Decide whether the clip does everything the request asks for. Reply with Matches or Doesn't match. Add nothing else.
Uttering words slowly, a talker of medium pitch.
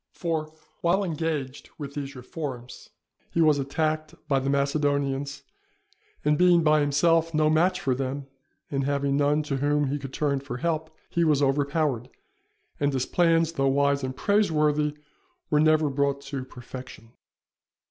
Doesn't match